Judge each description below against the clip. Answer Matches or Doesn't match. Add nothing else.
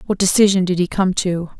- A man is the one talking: Doesn't match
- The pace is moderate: Doesn't match